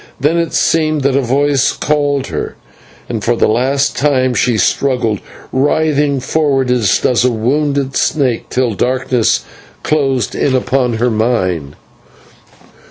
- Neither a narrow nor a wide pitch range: Yes, average, 3.0 semitones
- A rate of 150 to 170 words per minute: No, slow, 135 wpm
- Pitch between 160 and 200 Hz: No, low, 130 Hz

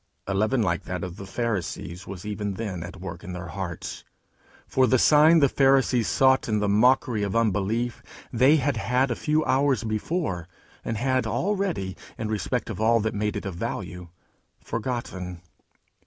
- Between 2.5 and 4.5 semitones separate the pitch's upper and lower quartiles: No, average, 5.2 semitones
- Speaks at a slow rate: No, average, 170 wpm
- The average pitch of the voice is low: Yes, low, 110 Hz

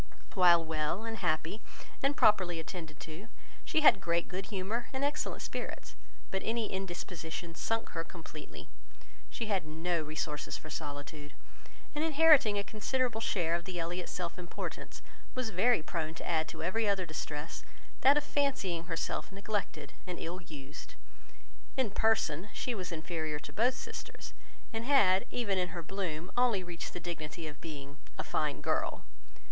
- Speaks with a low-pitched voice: No, medium, 180 Hz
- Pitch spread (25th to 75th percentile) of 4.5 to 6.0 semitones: Yes, average, 5.3 semitones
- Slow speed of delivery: No, average, 160 wpm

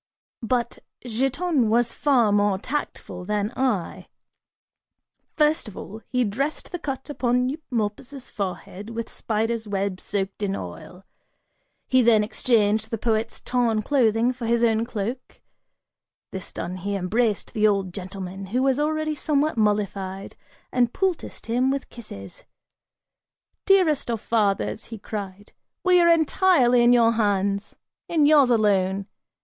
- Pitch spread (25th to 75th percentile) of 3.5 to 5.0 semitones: Yes, average, 4.2 semitones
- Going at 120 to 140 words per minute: Yes, slow, 135 wpm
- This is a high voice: Yes, high, 230 Hz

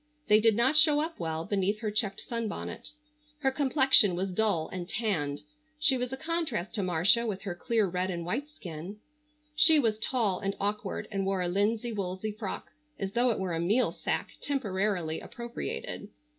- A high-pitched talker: Yes, high, 210 Hz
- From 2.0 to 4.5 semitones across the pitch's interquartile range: No, average, 4.9 semitones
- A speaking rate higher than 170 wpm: Yes, average, 180 wpm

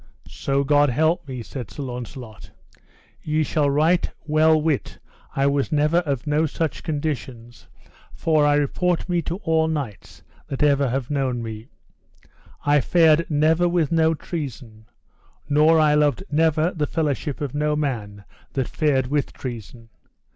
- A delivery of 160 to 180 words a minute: No, average, 145 wpm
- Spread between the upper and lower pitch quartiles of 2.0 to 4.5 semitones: Yes, average, 3.0 semitones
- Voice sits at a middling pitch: Yes, medium, 145 Hz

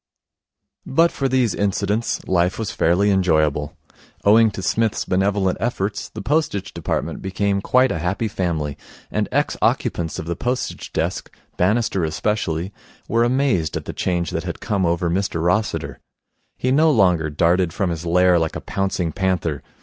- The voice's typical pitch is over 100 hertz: No, very low, 95 Hz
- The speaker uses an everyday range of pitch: Yes, average, 4.1 semitones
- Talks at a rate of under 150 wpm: No, average, 155 wpm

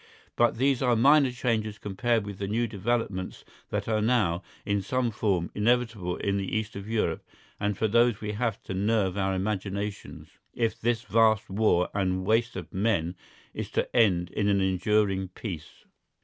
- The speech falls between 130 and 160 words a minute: No, average, 170 wpm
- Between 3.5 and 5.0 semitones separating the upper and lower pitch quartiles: No, average, 3.1 semitones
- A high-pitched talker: No, low, 105 Hz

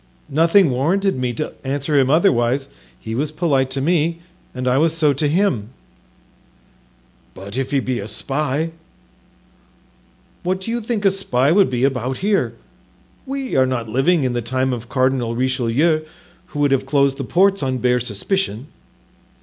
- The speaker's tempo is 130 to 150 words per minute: No, average, 165 wpm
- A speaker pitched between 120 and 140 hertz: Yes, low, 135 Hz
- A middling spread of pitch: Yes, average, 4.6 semitones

